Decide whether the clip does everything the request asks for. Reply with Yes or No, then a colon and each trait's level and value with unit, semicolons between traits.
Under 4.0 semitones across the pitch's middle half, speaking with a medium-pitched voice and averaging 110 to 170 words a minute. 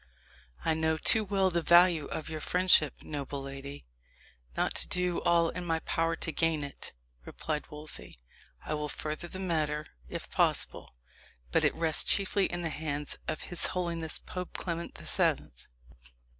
Yes: narrow, 2.6 semitones; medium, 160 Hz; average, 160 wpm